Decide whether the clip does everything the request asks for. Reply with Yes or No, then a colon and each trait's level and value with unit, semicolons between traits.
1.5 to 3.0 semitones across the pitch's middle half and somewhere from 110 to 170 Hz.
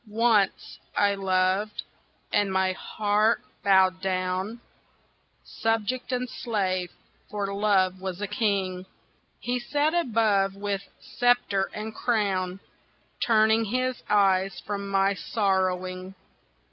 No: average, 2.7 semitones; high, 200 Hz